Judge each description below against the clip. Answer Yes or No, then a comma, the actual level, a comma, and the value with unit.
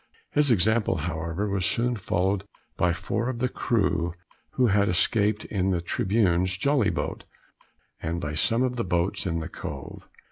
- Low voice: Yes, very low, 95 Hz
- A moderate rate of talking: Yes, average, 165 wpm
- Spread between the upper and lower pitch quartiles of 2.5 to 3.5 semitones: No, average, 4.9 semitones